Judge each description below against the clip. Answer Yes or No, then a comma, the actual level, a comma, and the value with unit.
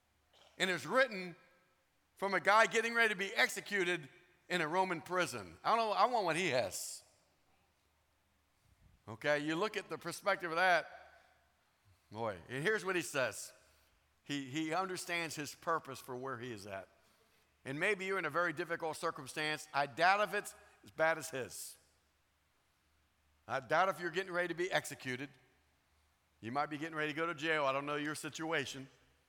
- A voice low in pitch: No, medium, 155 Hz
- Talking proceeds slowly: No, average, 175 wpm